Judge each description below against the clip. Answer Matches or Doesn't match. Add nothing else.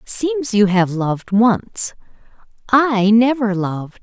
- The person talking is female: Matches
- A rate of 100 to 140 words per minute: Matches